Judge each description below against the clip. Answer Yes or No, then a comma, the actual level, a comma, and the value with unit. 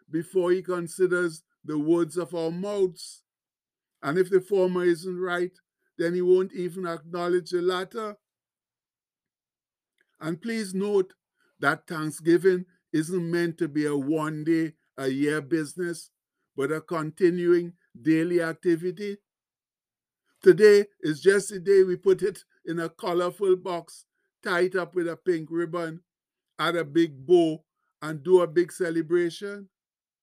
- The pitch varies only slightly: Yes, narrow, 2.1 semitones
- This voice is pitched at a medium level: Yes, medium, 175 Hz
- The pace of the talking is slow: Yes, slow, 130 wpm